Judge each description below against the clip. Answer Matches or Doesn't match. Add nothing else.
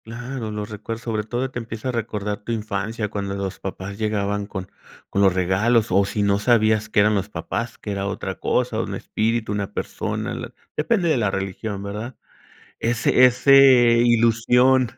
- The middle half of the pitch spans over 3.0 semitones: Doesn't match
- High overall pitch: Doesn't match